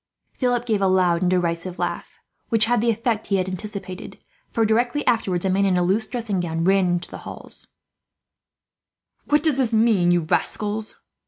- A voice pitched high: Yes, high, 200 Hz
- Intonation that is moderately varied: Yes, average, 4.1 semitones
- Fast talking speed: No, average, 180 wpm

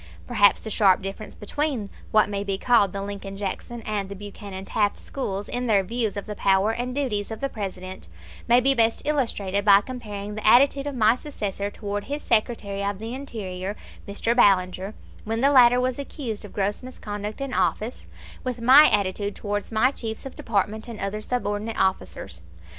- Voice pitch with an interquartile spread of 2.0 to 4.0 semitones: Yes, average, 3.4 semitones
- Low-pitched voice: No, high, 210 Hz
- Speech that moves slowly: No, average, 180 wpm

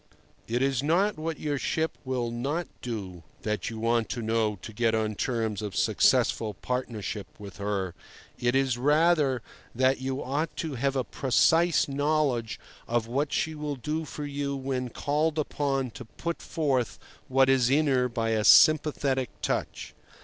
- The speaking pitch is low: Yes, low, 130 Hz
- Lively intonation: No, average, 4.2 semitones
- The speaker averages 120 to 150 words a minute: No, average, 165 wpm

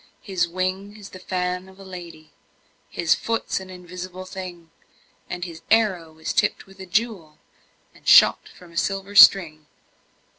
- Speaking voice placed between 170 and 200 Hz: Yes, medium, 185 Hz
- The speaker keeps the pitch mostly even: Yes, narrow, 2.0 semitones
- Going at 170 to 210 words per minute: No, average, 155 wpm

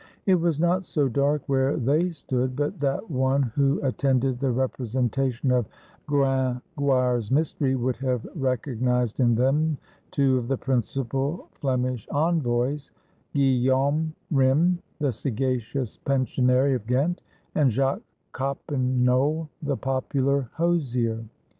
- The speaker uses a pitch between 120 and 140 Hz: Yes, low, 135 Hz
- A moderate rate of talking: No, slow, 120 wpm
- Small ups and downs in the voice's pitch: Yes, narrow, 2.1 semitones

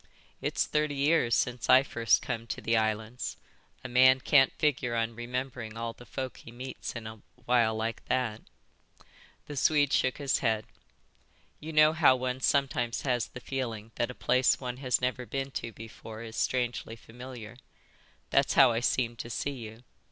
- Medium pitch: No, low, 125 Hz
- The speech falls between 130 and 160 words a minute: No, average, 175 wpm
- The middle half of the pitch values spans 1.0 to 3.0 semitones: Yes, narrow, 2.4 semitones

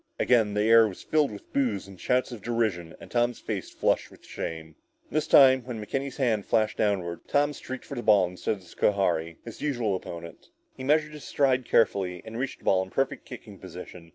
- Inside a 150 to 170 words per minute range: No, fast, 205 wpm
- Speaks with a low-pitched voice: Yes, low, 110 Hz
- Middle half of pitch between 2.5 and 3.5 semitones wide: No, wide, 5.6 semitones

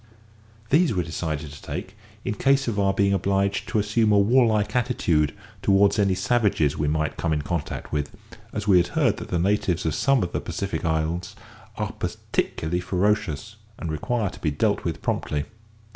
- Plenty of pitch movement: No, average, 4.8 semitones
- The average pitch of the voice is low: Yes, very low, 95 Hz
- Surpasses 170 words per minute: Yes, average, 180 wpm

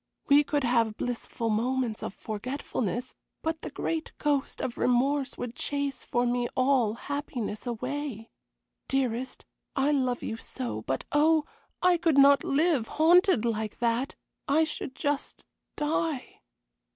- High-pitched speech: Yes, very high, 260 Hz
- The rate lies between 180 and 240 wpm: No, slow, 135 wpm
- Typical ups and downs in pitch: Yes, average, 3.8 semitones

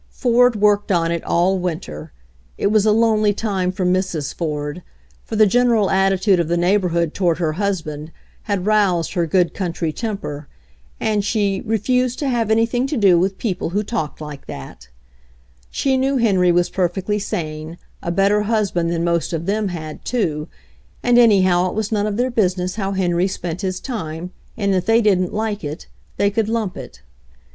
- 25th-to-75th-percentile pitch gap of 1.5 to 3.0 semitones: No, average, 3.8 semitones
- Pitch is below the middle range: No, high, 190 Hz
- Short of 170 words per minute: No, average, 175 wpm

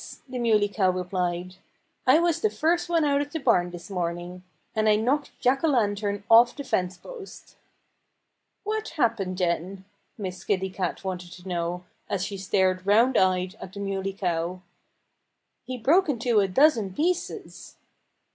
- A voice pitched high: Yes, high, 200 Hz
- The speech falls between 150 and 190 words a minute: Yes, average, 155 wpm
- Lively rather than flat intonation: Yes, wide, 6.1 semitones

